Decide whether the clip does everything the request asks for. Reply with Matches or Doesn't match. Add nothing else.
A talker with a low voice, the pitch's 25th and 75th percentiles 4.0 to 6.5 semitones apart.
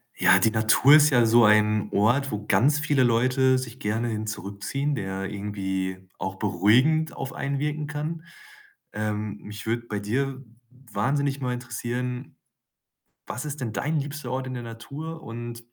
Matches